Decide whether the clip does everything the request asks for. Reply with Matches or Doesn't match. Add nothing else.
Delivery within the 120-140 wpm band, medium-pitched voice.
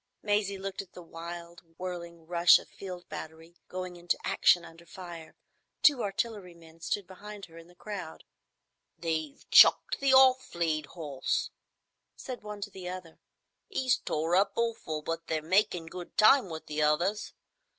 Doesn't match